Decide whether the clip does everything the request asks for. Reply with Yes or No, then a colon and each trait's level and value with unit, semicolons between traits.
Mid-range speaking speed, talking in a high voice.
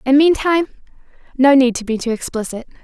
Yes: average, 150 wpm; very high, 265 Hz